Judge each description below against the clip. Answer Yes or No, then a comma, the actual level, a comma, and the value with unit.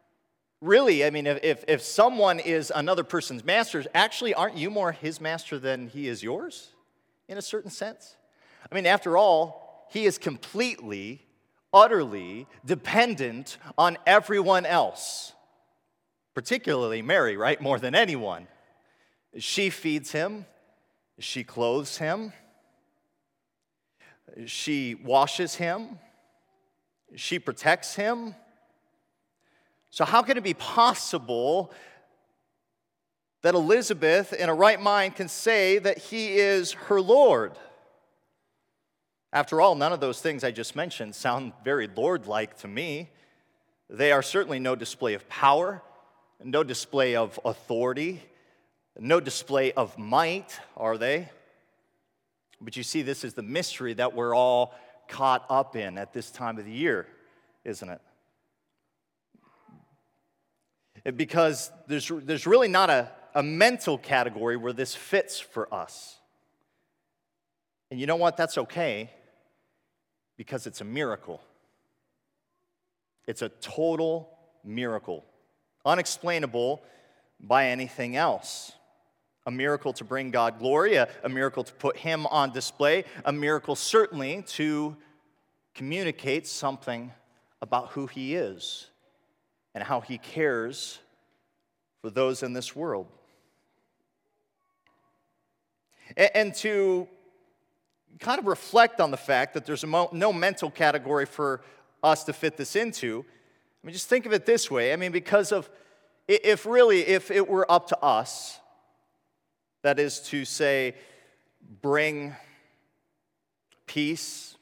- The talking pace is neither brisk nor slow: No, slow, 125 wpm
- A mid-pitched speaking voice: Yes, medium, 155 Hz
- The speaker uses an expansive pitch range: Yes, wide, 7.4 semitones